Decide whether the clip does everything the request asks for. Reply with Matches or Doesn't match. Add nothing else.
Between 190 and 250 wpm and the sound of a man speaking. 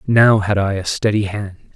Matches